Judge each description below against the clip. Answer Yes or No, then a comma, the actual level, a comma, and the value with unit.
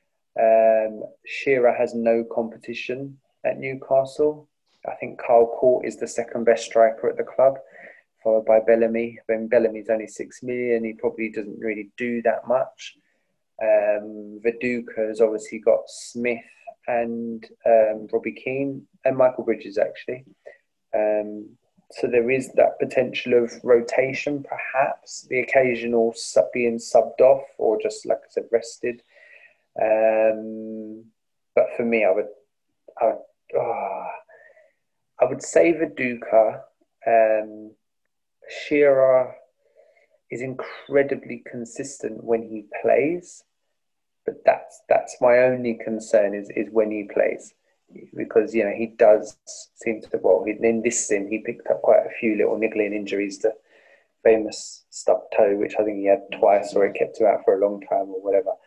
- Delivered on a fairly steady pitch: No, average, 3.5 semitones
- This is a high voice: No, low, 115 Hz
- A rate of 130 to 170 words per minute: Yes, average, 145 wpm